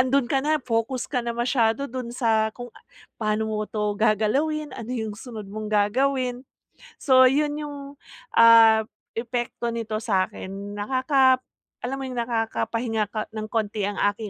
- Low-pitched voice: No, high, 230 Hz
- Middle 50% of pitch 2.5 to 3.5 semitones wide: Yes, average, 3.0 semitones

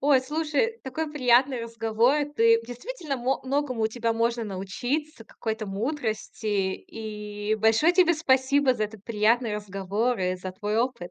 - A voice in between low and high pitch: No, high, 235 Hz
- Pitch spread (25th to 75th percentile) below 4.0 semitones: No, average, 4.3 semitones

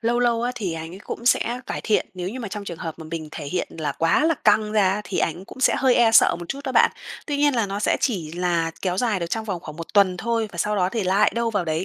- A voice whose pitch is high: Yes, high, 200 Hz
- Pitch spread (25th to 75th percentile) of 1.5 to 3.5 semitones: No, average, 5.2 semitones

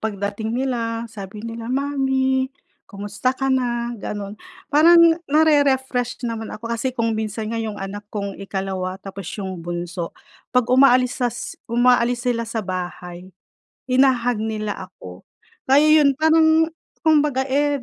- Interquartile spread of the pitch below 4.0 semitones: No, average, 4.4 semitones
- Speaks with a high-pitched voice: Yes, high, 235 Hz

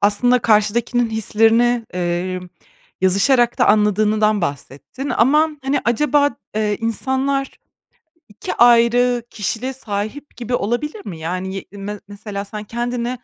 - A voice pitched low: No, high, 225 Hz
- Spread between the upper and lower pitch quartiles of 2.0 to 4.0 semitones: Yes, average, 3.2 semitones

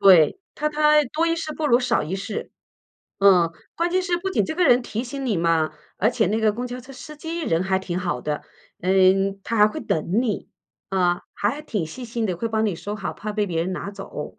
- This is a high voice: Yes, high, 215 Hz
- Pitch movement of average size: No, wide, 7.0 semitones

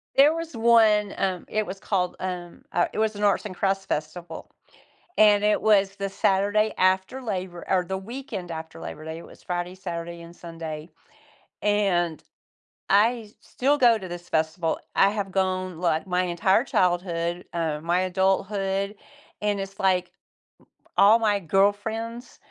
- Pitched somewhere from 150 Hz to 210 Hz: Yes, high, 190 Hz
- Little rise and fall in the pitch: No, average, 3.1 semitones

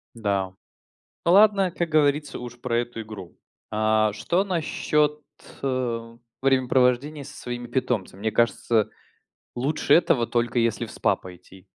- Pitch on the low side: Yes, low, 120 Hz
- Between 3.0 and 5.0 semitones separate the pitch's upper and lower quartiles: Yes, average, 4.7 semitones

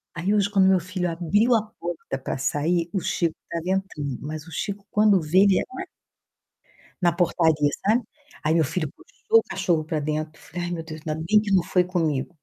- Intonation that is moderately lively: Yes, average, 3.6 semitones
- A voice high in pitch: No, medium, 175 Hz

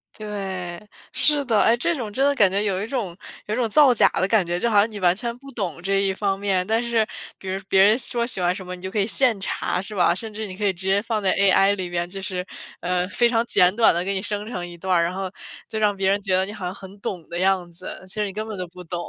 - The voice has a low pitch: No, high, 195 Hz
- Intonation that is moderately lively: Yes, average, 3.0 semitones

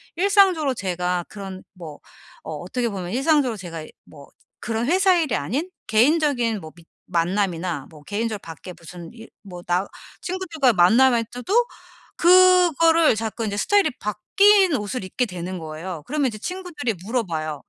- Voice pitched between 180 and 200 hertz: No, high, 225 Hz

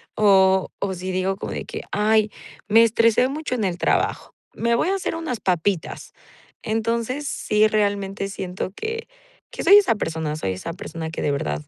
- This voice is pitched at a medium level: No, high, 205 Hz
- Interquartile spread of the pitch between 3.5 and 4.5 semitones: Yes, average, 4.0 semitones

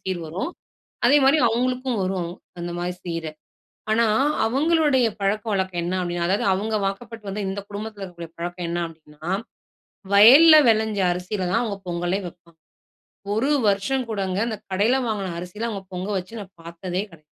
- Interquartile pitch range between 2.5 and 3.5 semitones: No, average, 4.0 semitones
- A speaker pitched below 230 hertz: Yes, high, 195 Hz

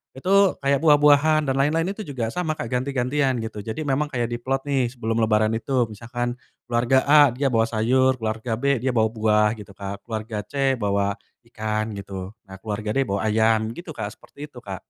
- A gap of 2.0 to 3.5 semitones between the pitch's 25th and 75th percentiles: No, average, 4.0 semitones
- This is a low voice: Yes, low, 120 Hz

